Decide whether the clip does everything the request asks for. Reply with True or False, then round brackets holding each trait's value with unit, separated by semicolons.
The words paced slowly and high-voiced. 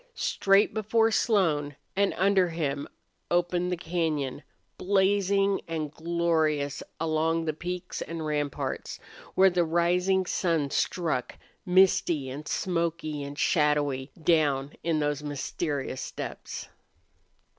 False (110 wpm; 165 Hz)